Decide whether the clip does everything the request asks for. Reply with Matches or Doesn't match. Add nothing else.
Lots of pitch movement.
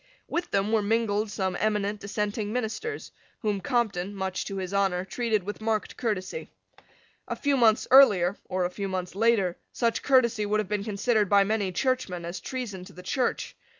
Doesn't match